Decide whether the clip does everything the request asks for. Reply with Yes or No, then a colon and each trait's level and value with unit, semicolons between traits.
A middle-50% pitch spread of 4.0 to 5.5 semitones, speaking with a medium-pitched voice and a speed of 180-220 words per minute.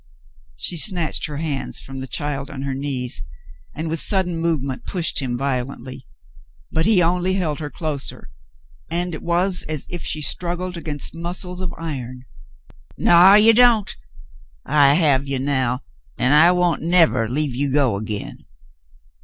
No: average, 4.6 semitones; medium, 155 Hz; average, 155 wpm